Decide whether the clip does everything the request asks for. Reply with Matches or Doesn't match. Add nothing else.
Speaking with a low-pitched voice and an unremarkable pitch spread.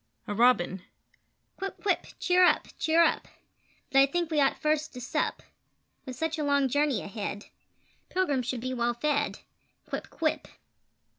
Doesn't match